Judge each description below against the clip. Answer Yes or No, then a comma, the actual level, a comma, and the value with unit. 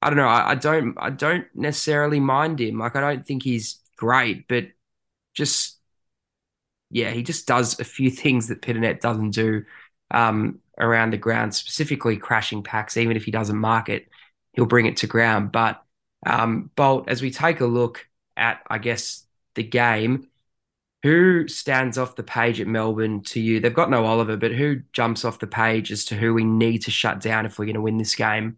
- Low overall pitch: Yes, low, 115 Hz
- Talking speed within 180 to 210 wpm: Yes, average, 200 wpm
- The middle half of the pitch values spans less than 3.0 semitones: Yes, narrow, 2.5 semitones